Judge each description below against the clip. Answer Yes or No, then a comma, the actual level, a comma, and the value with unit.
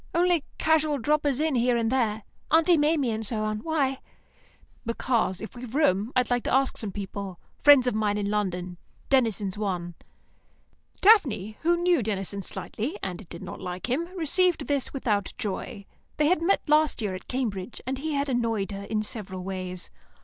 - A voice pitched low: No, high, 235 Hz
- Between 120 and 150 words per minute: No, average, 175 wpm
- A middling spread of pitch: No, wide, 6.4 semitones